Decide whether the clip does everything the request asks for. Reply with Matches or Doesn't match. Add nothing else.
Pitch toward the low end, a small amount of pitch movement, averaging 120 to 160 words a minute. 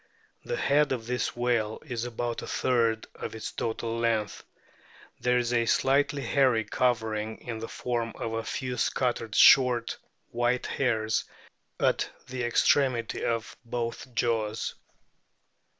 Matches